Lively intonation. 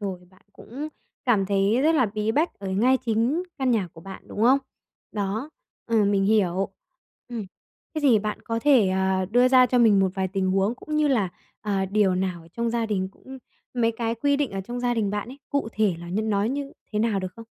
No: average, 4.1 semitones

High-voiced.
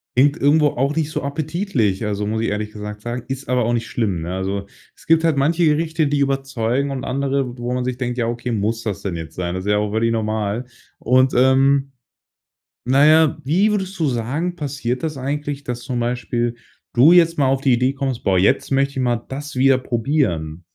No: low, 130 Hz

